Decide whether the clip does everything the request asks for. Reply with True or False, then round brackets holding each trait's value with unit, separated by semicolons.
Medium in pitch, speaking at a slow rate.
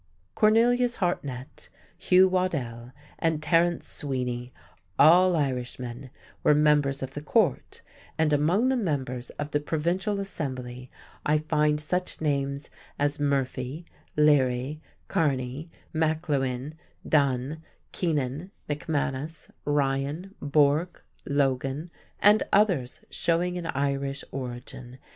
True (145 Hz; 105 wpm)